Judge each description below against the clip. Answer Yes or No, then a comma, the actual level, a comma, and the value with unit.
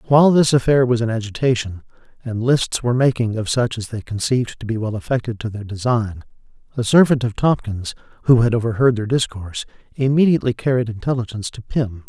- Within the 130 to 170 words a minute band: No, average, 180 wpm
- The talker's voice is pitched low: Yes, low, 120 Hz